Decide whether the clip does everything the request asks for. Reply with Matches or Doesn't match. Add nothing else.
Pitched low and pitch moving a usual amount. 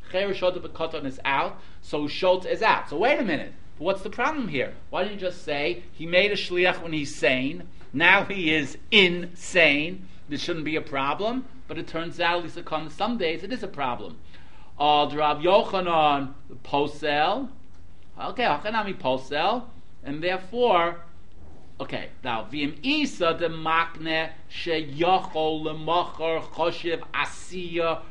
Doesn't match